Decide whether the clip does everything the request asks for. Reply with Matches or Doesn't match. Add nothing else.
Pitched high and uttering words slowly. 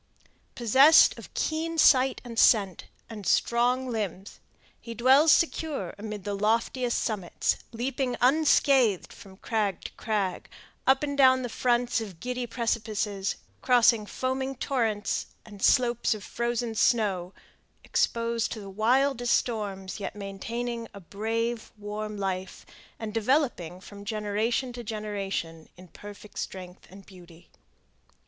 Matches